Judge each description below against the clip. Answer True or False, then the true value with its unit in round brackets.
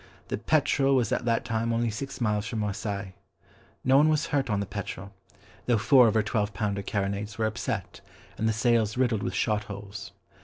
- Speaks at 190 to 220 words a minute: True (195 wpm)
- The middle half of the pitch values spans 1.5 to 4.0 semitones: True (2.8 semitones)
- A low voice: True (110 Hz)